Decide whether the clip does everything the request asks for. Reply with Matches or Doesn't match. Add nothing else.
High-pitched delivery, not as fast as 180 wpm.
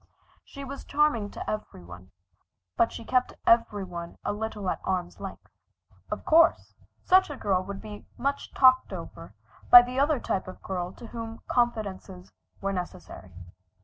Matches